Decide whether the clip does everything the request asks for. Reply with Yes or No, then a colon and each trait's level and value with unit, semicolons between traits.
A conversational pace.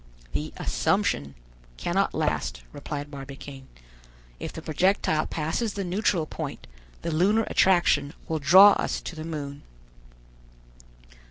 No: slow, 115 wpm